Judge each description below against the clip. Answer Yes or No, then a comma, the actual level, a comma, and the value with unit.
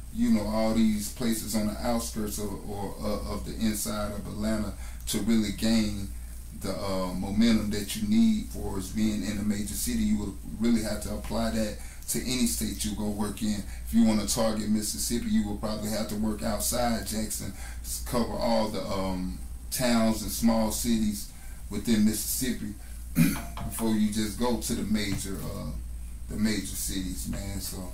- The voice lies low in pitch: Yes, low, 105 Hz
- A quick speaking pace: No, average, 175 wpm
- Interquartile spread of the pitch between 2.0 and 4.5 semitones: Yes, narrow, 2.5 semitones